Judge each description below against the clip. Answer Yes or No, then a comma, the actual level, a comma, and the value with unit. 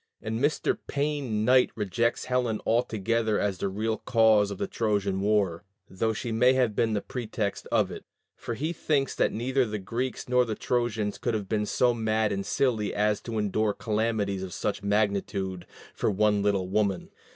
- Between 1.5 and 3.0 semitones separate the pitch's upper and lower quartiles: Yes, narrow, 2.6 semitones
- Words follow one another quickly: No, average, 180 wpm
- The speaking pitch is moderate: No, low, 110 Hz